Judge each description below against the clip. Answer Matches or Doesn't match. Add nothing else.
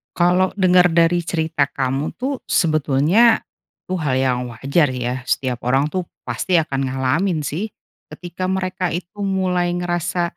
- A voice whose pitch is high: Doesn't match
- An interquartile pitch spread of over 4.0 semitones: Matches